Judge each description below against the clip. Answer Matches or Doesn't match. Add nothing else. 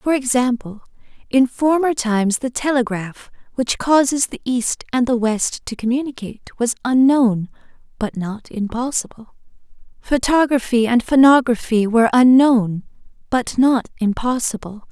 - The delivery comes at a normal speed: Doesn't match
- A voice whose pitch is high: Matches